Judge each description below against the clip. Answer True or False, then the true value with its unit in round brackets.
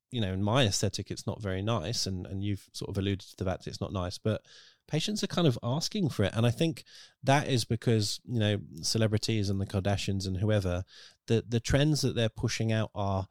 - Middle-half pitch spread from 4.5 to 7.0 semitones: False (3.5 semitones)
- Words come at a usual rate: False (230 wpm)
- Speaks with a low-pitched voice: True (110 Hz)